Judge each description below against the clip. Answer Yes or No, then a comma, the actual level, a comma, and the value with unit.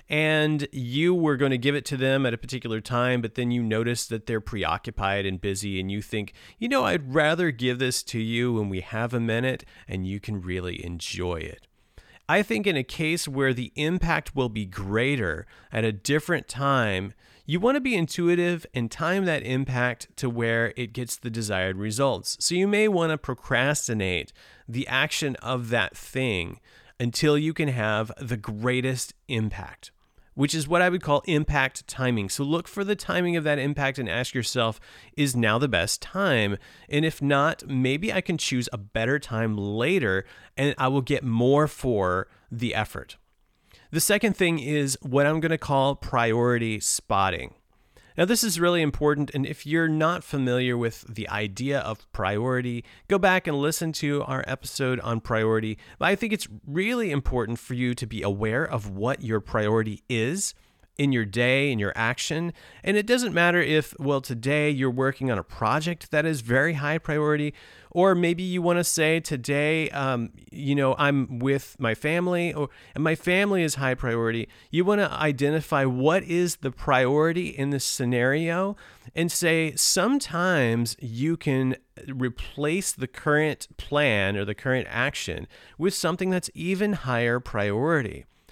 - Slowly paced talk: No, average, 175 wpm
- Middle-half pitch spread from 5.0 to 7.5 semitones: Yes, average, 5.3 semitones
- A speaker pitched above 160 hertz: No, low, 135 Hz